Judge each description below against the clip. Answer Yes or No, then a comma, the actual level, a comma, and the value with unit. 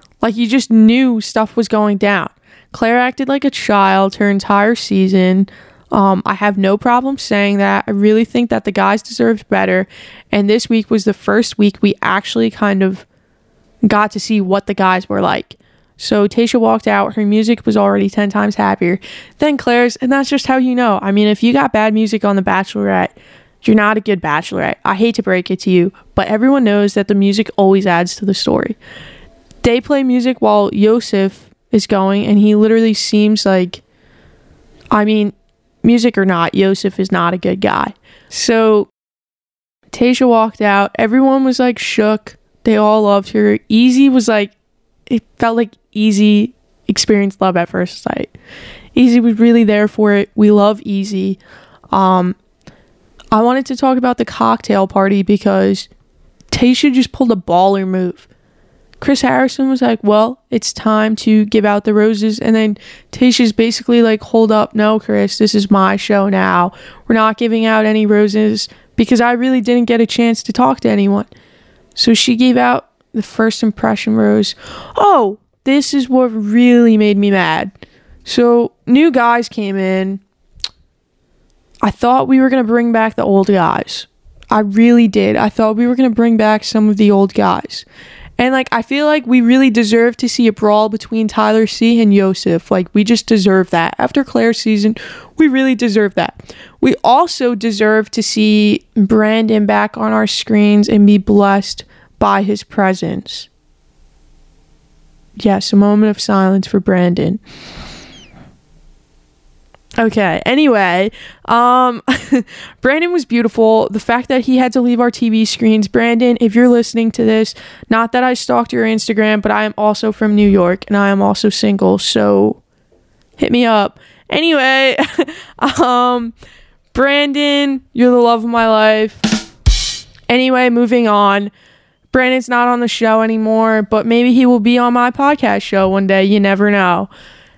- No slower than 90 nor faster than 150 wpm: No, average, 170 wpm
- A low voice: No, high, 220 Hz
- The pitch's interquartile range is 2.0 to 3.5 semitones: Yes, average, 3.0 semitones